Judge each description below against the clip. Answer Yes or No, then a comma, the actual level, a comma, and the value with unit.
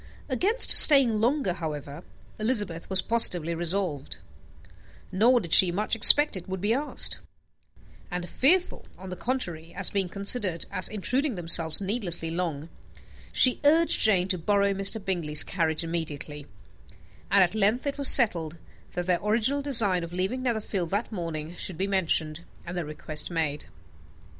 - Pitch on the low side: No, high, 190 Hz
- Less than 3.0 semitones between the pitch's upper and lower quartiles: No, average, 5.0 semitones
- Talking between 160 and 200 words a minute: No, average, 150 wpm